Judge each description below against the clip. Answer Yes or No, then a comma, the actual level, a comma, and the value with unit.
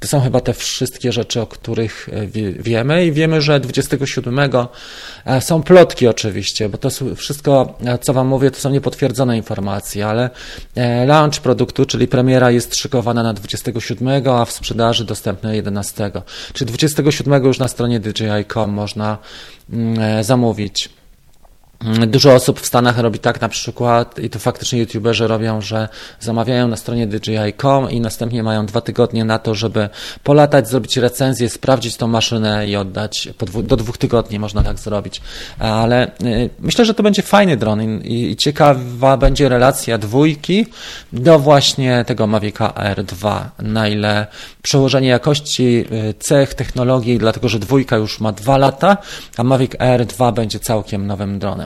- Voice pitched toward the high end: No, low, 120 Hz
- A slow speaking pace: No, average, 145 wpm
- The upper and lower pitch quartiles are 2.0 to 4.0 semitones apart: Yes, average, 3.5 semitones